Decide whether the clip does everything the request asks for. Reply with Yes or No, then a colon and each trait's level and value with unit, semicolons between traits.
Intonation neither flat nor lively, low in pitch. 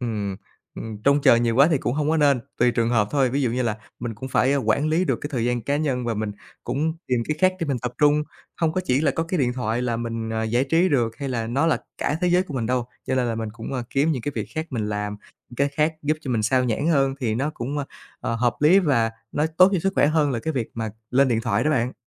Yes: average, 4.2 semitones; low, 130 Hz